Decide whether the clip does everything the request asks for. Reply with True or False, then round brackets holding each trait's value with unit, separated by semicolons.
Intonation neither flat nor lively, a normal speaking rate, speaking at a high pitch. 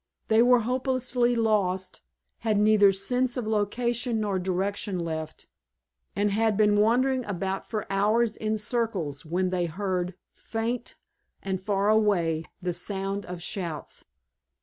False (3.4 semitones; 130 wpm; 205 Hz)